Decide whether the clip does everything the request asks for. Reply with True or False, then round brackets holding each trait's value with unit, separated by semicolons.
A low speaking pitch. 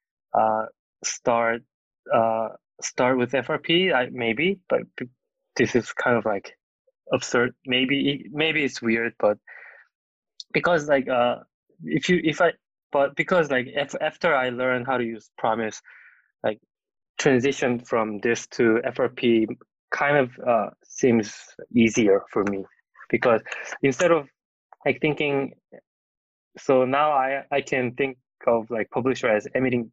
True (130 Hz)